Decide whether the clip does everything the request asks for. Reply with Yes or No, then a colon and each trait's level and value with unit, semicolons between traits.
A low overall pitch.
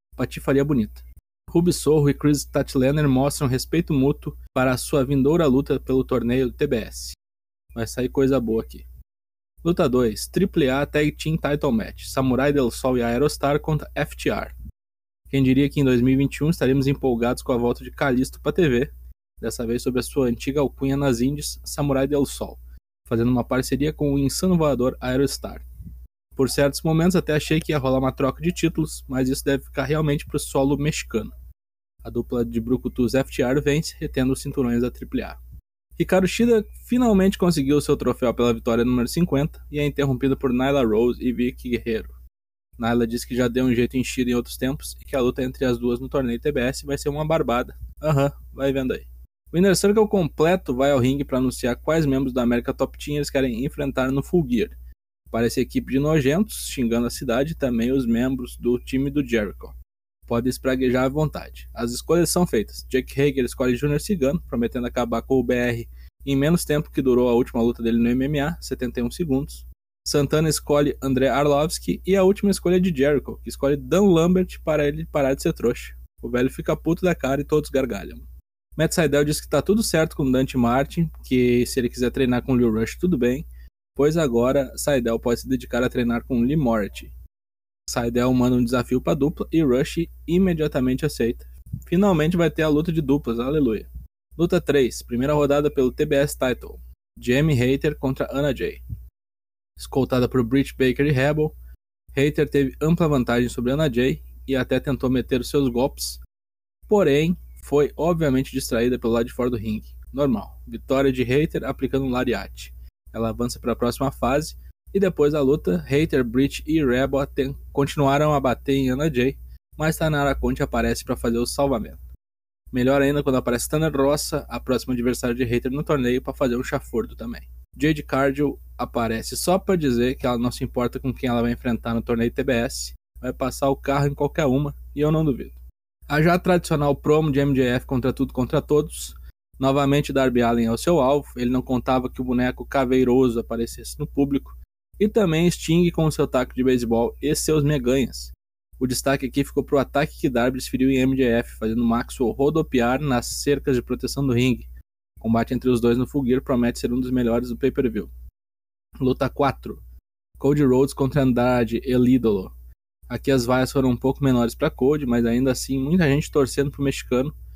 Yes: low, 130 Hz